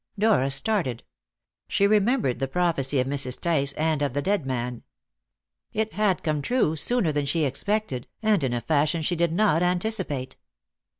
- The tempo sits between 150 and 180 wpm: Yes, average, 165 wpm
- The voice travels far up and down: Yes, wide, 6.7 semitones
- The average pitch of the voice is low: No, medium, 160 Hz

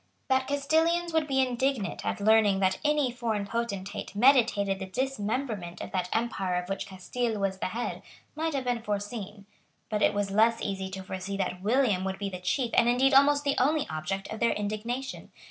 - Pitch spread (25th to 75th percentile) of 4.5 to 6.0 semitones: Yes, average, 5.1 semitones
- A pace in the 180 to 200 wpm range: Yes, average, 190 wpm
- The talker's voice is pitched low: No, high, 220 Hz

